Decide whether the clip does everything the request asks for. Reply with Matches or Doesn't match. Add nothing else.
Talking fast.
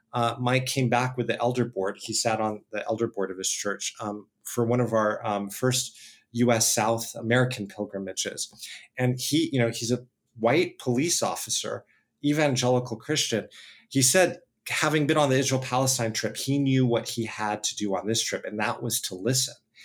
Doesn't match